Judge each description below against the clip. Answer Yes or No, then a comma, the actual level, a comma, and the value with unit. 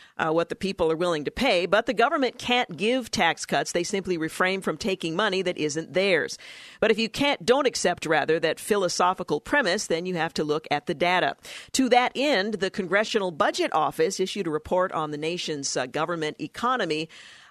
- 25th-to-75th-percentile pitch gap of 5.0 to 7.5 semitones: Yes, average, 5.3 semitones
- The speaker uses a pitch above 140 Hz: Yes, medium, 185 Hz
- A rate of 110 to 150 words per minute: No, average, 200 wpm